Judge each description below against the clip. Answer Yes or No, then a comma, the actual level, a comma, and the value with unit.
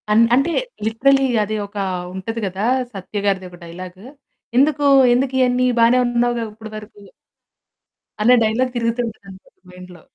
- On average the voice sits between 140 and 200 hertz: No, high, 225 Hz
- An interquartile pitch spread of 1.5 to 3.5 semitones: No, average, 4.1 semitones